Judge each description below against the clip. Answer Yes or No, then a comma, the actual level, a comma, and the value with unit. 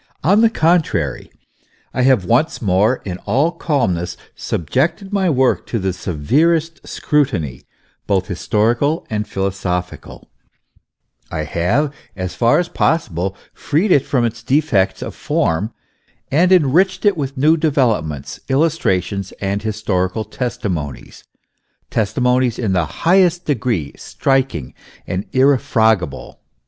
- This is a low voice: Yes, low, 120 Hz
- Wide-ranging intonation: Yes, wide, 8.1 semitones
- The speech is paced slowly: Yes, slow, 120 wpm